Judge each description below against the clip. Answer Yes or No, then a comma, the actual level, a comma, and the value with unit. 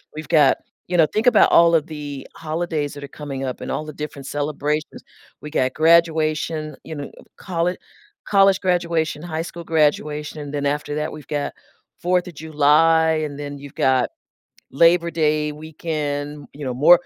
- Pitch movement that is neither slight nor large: No, narrow, 2.2 semitones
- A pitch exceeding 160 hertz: No, medium, 155 Hz